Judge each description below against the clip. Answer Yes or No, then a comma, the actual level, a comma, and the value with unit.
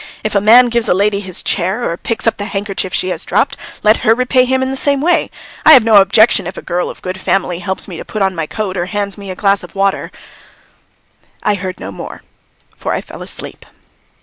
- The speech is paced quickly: Yes, fast, 240 wpm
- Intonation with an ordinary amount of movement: Yes, average, 3.4 semitones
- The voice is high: Yes, high, 200 Hz